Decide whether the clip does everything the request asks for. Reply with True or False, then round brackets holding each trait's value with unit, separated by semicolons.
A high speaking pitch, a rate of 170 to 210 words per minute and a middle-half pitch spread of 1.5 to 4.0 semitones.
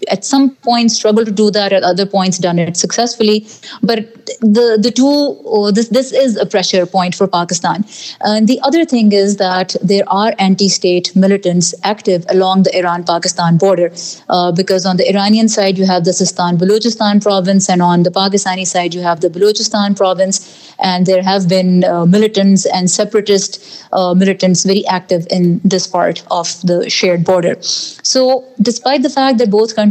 True (195 Hz; 175 wpm; 2.9 semitones)